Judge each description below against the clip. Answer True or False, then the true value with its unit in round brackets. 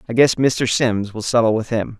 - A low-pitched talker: True (115 Hz)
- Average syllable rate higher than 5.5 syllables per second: False (5.0 syllables/s)